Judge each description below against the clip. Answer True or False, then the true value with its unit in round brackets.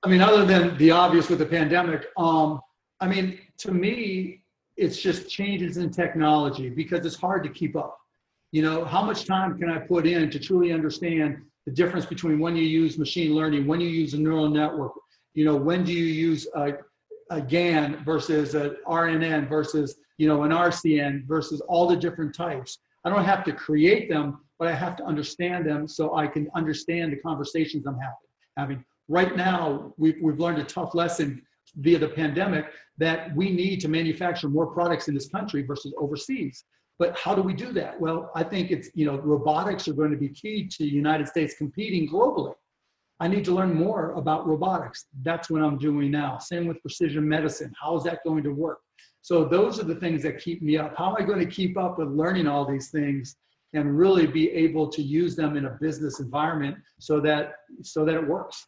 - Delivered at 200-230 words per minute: True (205 wpm)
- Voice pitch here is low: False (160 Hz)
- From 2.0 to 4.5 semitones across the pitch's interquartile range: True (2.4 semitones)